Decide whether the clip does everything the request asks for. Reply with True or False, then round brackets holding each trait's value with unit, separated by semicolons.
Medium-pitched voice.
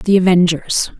True (180 Hz)